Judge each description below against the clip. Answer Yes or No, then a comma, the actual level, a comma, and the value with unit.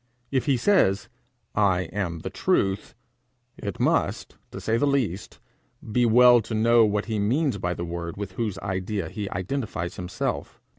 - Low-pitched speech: Yes, low, 105 Hz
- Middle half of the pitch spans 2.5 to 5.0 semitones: Yes, average, 3.9 semitones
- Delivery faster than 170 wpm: No, average, 160 wpm